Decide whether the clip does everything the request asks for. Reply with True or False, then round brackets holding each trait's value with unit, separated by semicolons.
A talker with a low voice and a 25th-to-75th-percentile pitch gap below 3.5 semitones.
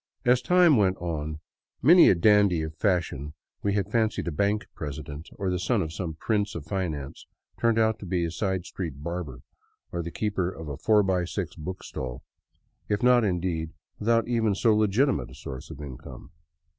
False (95 Hz; 5.0 semitones)